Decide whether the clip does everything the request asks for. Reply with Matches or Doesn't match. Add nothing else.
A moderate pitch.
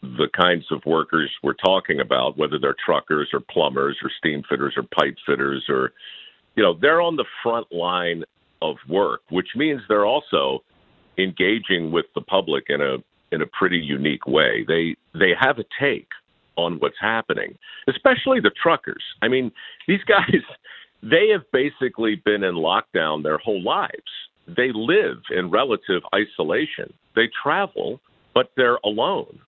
Doesn't match